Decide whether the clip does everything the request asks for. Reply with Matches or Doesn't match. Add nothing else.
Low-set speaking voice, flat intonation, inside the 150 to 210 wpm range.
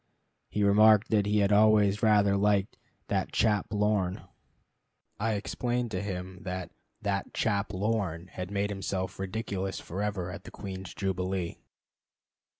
Doesn't match